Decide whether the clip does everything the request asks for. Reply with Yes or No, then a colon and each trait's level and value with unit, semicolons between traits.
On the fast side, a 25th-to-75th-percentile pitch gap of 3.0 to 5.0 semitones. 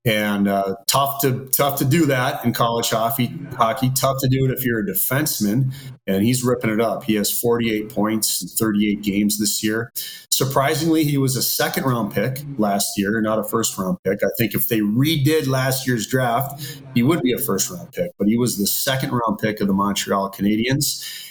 Yes: fast, 210 wpm; average, 4.2 semitones